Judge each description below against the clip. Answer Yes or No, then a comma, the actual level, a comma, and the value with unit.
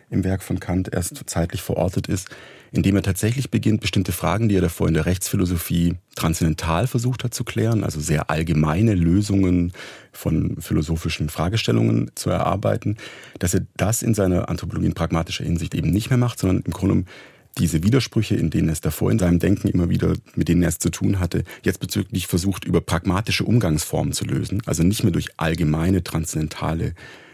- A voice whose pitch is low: Yes, very low, 95 Hz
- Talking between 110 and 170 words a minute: No, average, 180 wpm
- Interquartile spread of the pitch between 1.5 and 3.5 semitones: No, average, 4.0 semitones